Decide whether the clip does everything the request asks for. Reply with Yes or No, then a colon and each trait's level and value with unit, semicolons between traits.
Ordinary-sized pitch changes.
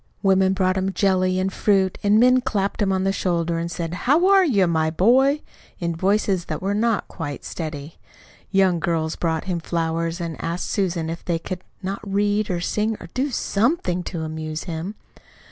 Yes: average, 3.4 semitones